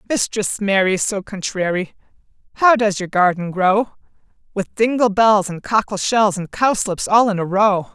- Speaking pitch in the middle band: No, high, 200 Hz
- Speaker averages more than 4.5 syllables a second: No, 4.4 syllables/s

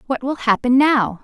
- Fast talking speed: No, average, 195 wpm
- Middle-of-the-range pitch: No, very high, 250 Hz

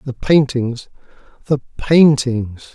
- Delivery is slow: Yes, slow, 65 wpm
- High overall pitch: No, low, 130 Hz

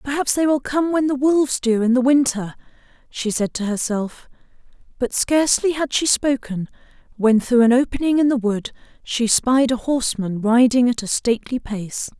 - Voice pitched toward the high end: Yes, very high, 250 Hz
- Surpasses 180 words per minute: No, average, 175 wpm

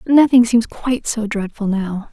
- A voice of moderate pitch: No, high, 225 Hz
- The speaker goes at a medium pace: Yes, average, 170 wpm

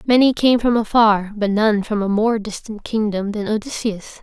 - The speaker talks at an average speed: Yes, average, 185 wpm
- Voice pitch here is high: Yes, high, 215 Hz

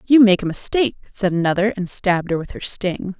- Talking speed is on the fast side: Yes, fast, 225 wpm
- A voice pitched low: No, high, 195 Hz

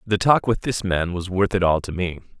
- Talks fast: Yes, fast, 275 wpm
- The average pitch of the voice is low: Yes, very low, 95 Hz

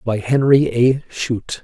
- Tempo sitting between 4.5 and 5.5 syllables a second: No, 4.1 syllables/s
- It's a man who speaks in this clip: Yes, male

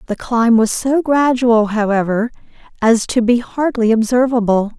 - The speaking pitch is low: No, high, 235 Hz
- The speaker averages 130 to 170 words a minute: Yes, average, 140 wpm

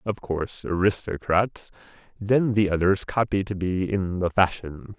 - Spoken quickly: No, average, 145 wpm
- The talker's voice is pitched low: Yes, very low, 95 Hz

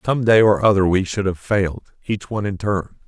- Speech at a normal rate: No, fast, 235 wpm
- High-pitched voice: No, low, 100 Hz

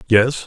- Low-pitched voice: Yes, low, 120 Hz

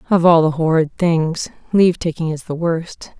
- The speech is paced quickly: No, average, 170 wpm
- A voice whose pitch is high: No, medium, 165 Hz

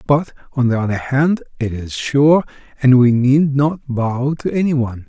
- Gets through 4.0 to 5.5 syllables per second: Yes, 4.5 syllables/s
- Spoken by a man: Yes, male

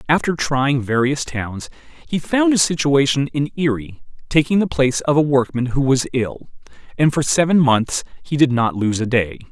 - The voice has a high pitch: No, low, 135 Hz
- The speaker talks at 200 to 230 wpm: No, average, 185 wpm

